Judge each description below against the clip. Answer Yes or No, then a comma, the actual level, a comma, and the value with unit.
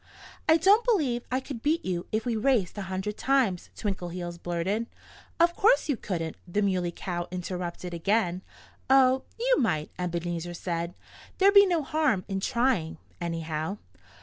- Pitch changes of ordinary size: No, wide, 7.4 semitones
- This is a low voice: No, high, 195 Hz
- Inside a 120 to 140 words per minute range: No, average, 150 wpm